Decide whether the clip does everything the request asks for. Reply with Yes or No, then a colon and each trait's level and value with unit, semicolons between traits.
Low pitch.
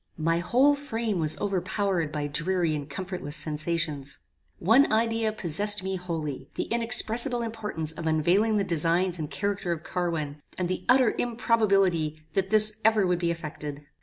No: medium, 180 Hz